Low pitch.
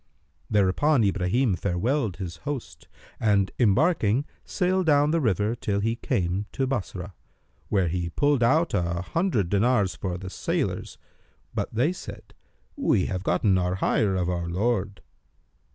Yes: low, 100 Hz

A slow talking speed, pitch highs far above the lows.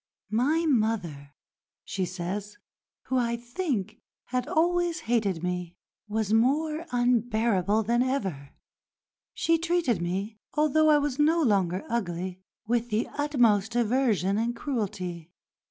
Yes: slow, 120 wpm; wide, 5.9 semitones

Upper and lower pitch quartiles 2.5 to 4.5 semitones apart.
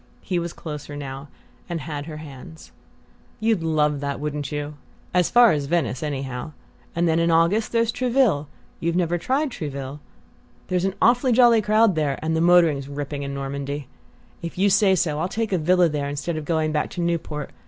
Yes: average, 4.0 semitones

